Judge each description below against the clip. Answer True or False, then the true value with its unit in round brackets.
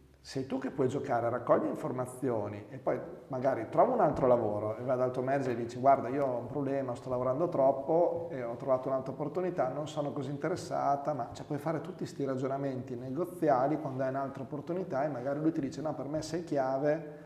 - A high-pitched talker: False (135 Hz)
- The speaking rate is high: True (210 wpm)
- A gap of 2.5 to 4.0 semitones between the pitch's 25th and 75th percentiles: True (2.8 semitones)